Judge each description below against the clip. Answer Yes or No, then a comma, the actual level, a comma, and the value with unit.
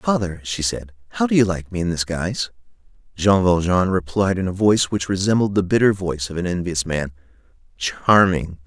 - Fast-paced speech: No, average, 185 wpm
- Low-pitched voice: Yes, very low, 90 Hz